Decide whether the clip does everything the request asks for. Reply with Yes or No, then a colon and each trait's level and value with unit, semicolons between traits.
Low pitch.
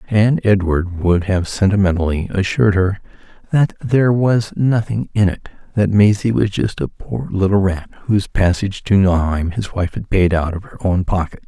Yes: low, 100 Hz